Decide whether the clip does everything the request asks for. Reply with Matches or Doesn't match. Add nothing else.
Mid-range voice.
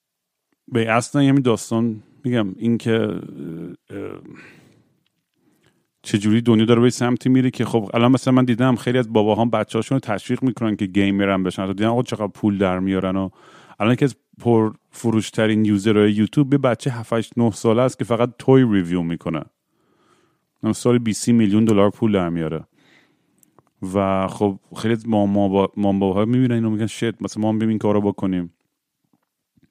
Doesn't match